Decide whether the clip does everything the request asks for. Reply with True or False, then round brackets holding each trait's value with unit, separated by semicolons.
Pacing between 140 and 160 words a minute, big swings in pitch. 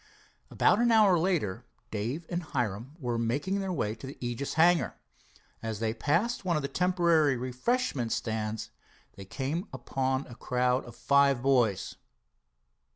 True (150 wpm; 6.4 semitones)